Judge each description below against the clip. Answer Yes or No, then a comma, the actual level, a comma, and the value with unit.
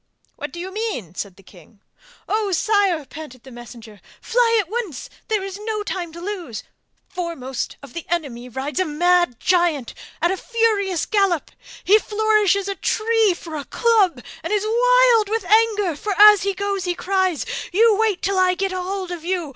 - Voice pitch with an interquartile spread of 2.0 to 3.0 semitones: No, average, 4.9 semitones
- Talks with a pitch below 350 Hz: No, very high, 375 Hz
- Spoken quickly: No, average, 180 wpm